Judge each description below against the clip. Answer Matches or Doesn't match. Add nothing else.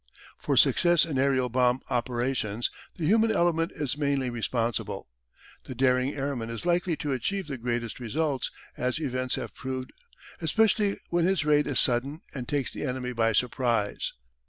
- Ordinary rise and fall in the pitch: Matches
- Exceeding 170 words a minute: Doesn't match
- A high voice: Doesn't match